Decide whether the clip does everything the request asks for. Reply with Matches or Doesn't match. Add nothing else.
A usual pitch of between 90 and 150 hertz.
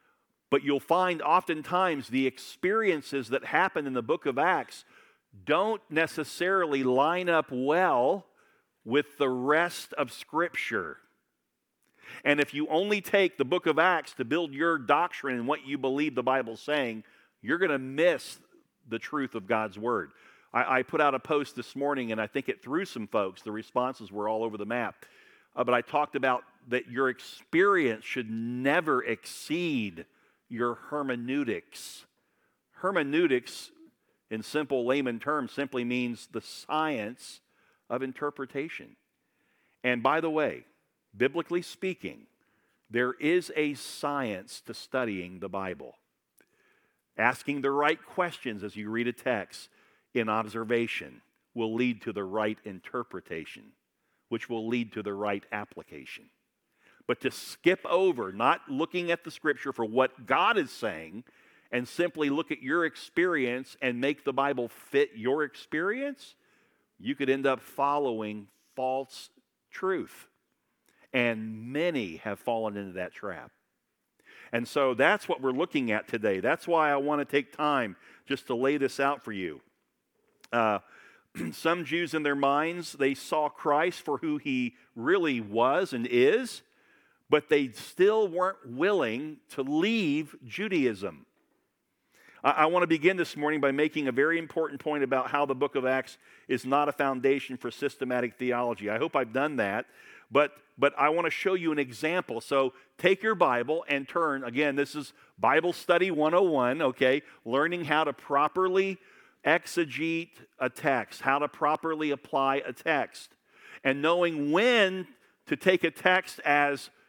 Matches